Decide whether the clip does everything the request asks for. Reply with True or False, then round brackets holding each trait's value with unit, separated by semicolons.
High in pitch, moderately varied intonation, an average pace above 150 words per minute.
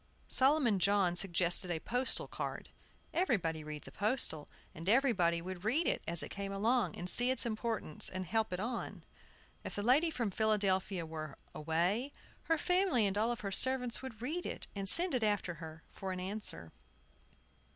False (205 Hz; 5.7 semitones; 170 wpm)